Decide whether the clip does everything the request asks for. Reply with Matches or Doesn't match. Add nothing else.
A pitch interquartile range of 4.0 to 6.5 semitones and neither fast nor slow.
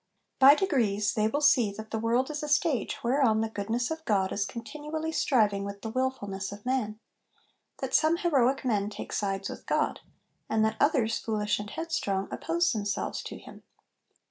Matches